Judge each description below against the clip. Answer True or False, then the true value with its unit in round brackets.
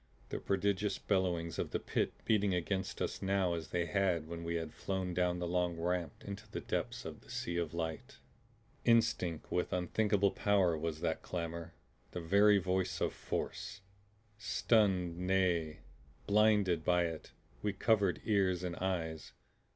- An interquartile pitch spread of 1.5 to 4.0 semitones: True (2.9 semitones)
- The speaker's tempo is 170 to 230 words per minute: False (155 wpm)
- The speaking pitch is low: True (90 Hz)